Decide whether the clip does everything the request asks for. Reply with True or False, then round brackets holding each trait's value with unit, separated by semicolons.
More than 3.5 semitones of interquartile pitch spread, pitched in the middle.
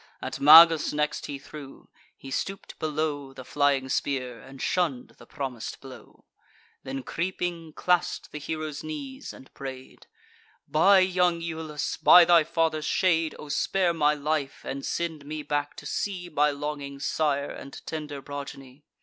False (3.1 semitones; 150 Hz)